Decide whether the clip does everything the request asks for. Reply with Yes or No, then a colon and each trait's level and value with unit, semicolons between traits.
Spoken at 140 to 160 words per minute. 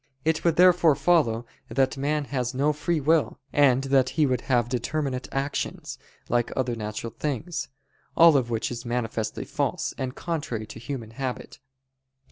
Yes: average, 155 wpm